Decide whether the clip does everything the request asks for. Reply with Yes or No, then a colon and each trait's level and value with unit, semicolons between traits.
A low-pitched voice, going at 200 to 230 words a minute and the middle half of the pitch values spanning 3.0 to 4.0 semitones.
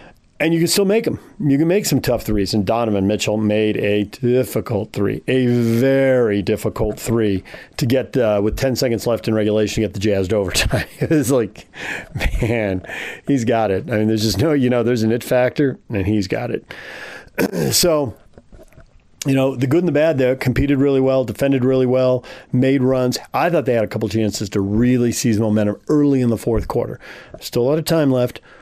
Yes: low, 120 Hz; fast, 205 wpm; average, 3.7 semitones